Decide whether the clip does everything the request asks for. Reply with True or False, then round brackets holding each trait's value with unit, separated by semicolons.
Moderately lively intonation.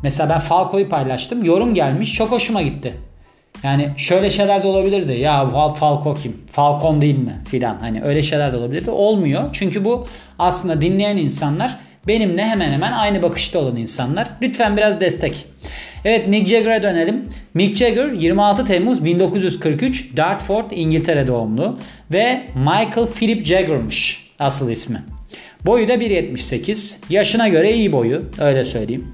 False (6.4 semitones)